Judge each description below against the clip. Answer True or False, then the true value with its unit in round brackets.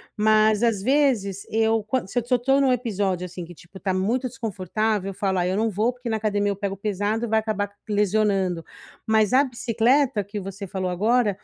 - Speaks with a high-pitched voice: True (210 Hz)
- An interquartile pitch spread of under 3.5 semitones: True (2.9 semitones)